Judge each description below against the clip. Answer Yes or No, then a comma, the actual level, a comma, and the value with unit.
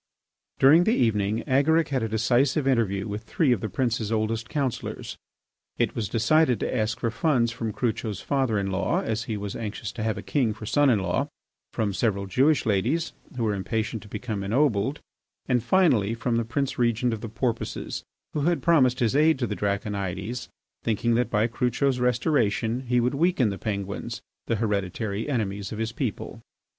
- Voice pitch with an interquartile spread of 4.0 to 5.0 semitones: No, average, 3.5 semitones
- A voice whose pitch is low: Yes, low, 115 Hz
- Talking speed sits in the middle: Yes, average, 185 wpm